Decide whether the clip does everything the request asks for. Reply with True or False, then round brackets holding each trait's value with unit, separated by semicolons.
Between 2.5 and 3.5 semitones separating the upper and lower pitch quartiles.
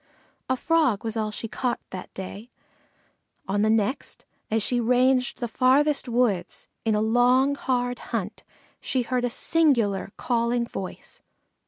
True (2.8 semitones)